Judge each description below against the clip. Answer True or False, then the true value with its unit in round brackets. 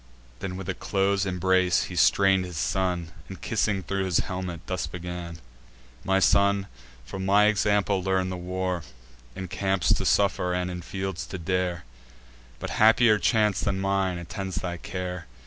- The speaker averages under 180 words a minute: True (160 wpm)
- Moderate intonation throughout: False (1.4 semitones)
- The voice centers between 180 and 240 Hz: False (95 Hz)